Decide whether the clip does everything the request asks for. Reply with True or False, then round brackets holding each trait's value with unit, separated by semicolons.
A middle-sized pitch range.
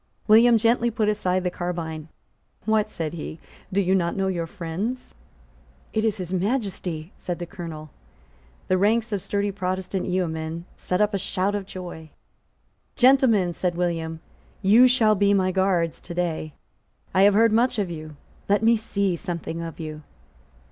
True (3.7 semitones)